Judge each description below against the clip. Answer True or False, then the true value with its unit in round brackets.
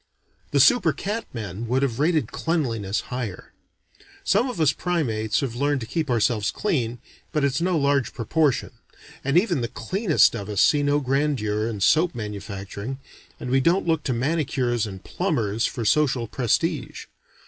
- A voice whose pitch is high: False (135 Hz)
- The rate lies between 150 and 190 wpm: True (160 wpm)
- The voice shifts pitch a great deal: True (5.7 semitones)